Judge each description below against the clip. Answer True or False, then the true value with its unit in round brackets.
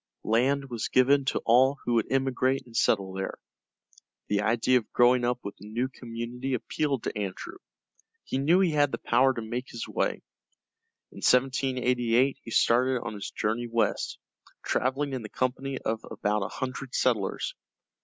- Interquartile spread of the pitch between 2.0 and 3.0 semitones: True (2.5 semitones)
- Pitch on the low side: True (125 Hz)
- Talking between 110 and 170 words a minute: True (165 wpm)